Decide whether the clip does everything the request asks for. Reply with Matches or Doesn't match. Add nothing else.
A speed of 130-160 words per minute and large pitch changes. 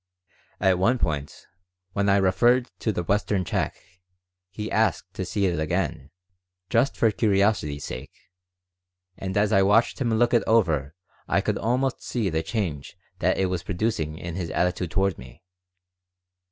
Doesn't match